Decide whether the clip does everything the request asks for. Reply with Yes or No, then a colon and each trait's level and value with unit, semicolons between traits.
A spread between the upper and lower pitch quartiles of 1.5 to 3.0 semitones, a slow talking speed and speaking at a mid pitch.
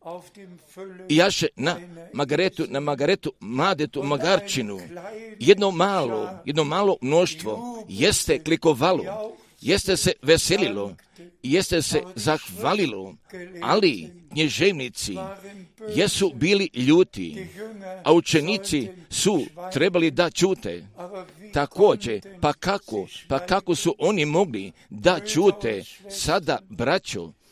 No: average, 4.0 semitones; slow, 95 wpm; medium, 175 Hz